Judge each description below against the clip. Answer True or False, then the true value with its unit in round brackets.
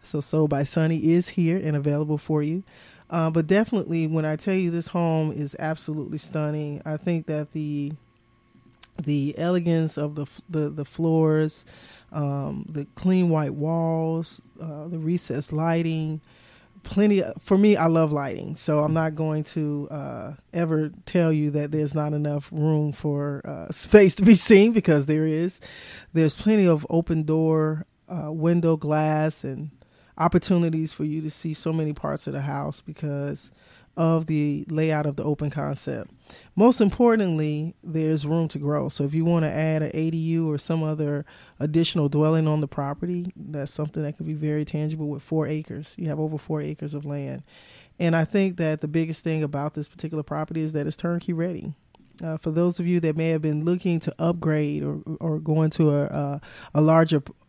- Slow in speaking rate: False (185 wpm)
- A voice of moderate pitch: True (155 Hz)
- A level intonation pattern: True (1.8 semitones)